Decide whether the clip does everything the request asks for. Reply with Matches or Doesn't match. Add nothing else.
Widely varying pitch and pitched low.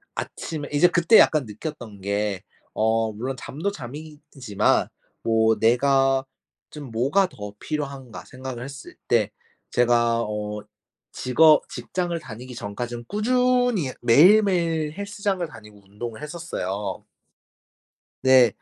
Matches